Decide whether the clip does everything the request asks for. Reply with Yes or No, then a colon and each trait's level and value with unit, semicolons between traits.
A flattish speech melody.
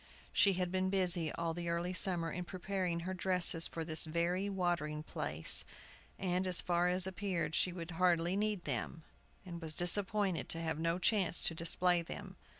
Yes: narrow, 1.9 semitones